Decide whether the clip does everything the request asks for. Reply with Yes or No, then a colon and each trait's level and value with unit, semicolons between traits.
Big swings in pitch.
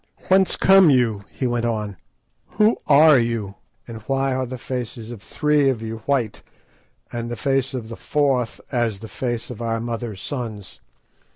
No: average, 3.1 semitones